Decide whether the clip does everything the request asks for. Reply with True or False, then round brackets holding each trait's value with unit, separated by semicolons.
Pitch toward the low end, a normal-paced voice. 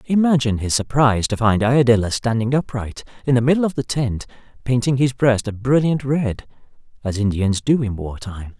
True (120 Hz; 180 wpm)